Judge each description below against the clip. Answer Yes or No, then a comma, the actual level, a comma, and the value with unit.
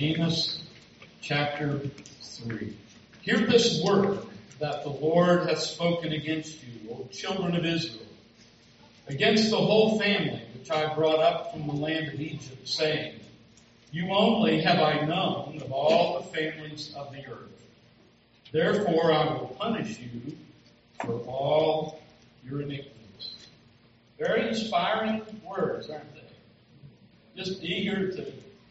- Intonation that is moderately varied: No, wide, 6.1 semitones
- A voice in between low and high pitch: Yes, medium, 155 Hz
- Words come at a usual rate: No, slow, 125 wpm